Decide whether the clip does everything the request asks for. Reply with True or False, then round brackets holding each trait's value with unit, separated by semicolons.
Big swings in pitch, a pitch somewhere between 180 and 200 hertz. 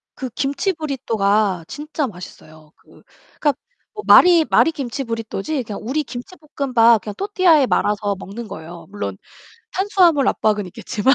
False (6.9 semitones; 245 Hz)